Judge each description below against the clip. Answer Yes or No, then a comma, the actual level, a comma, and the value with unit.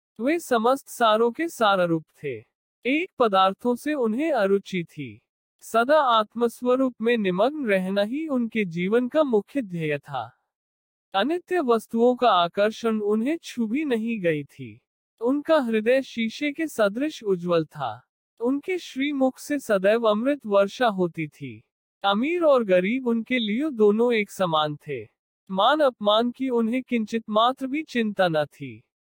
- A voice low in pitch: No, high, 230 Hz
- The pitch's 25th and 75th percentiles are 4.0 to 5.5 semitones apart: Yes, average, 5.2 semitones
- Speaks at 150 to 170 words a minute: No, average, 140 wpm